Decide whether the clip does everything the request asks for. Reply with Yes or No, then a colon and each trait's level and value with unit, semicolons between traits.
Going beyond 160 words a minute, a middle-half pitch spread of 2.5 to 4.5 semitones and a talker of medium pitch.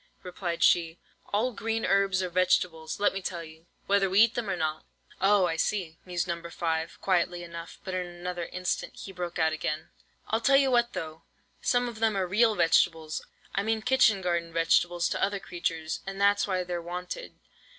Yes: average, 190 wpm; average, 3.1 semitones; medium, 180 Hz